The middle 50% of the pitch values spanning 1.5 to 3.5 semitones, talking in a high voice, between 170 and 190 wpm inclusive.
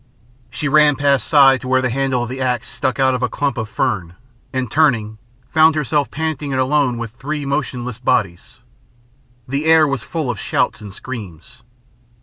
No: average, 2.9 semitones; low, 130 Hz; average, 180 wpm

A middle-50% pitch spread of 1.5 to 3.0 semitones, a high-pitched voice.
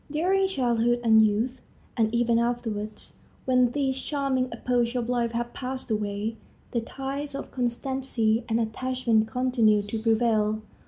Yes: average, 2.7 semitones; high, 240 Hz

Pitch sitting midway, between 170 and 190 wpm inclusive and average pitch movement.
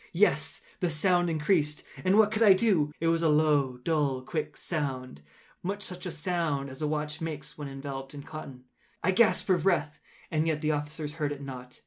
Yes: medium, 150 Hz; average, 180 wpm; average, 3.5 semitones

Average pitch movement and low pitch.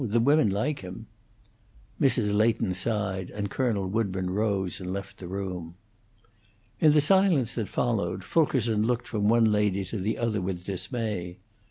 Yes: average, 3.7 semitones; low, 105 Hz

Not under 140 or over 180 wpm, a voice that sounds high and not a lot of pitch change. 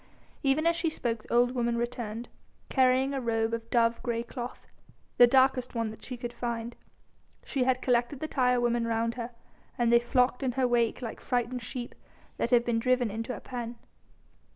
No: average, 190 wpm; high, 240 Hz; narrow, 1.4 semitones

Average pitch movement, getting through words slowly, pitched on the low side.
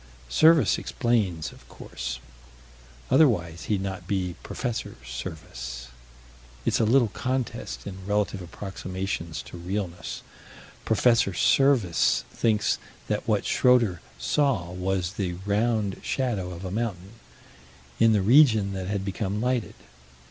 Yes: average, 4.6 semitones; slow, 120 wpm; low, 100 Hz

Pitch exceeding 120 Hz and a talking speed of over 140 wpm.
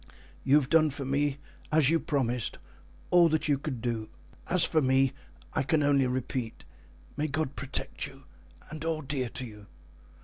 Yes: medium, 140 Hz; average, 170 wpm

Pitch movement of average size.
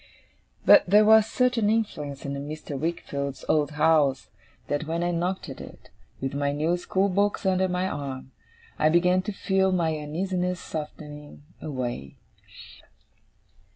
Yes: average, 4.4 semitones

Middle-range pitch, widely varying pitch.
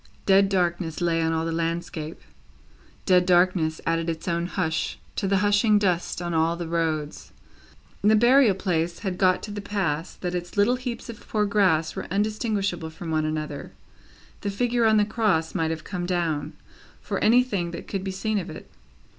No: medium, 180 Hz; average, 3.8 semitones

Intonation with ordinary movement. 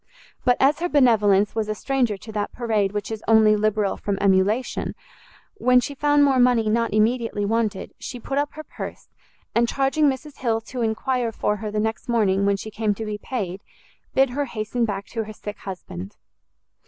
Yes: average, 3.3 semitones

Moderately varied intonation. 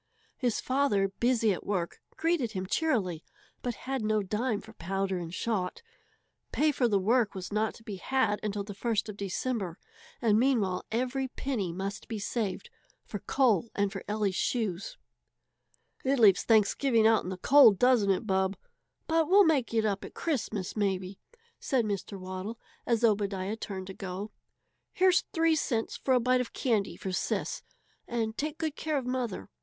Yes: average, 4.5 semitones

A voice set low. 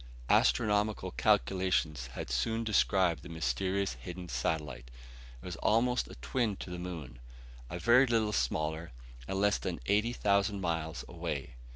Yes: very low, 90 Hz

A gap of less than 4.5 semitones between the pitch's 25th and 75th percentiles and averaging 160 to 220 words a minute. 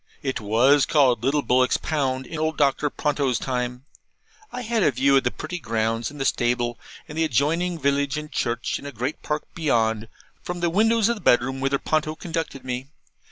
Yes: average, 4.0 semitones; average, 195 wpm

